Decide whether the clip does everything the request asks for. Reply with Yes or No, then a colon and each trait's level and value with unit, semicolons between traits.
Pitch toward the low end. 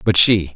Yes: very low, 90 Hz